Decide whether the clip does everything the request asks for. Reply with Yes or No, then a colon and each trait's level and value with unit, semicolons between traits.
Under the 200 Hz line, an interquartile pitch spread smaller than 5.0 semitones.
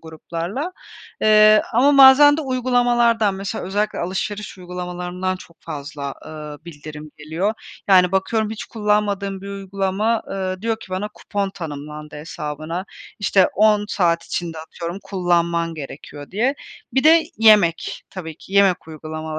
Yes: high, 190 Hz; average, 4.4 semitones